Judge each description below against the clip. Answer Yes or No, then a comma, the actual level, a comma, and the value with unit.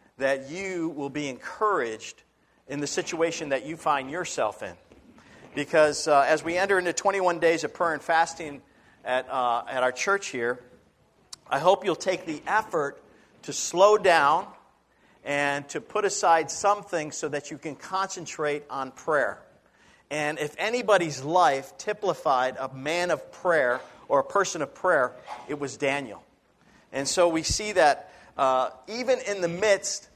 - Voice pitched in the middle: Yes, medium, 160 Hz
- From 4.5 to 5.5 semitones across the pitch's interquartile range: Yes, average, 4.9 semitones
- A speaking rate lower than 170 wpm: Yes, average, 155 wpm